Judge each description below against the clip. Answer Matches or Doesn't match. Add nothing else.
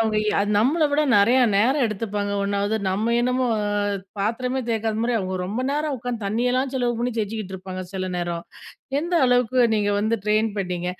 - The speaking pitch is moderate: Doesn't match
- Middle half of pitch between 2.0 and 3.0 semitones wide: Doesn't match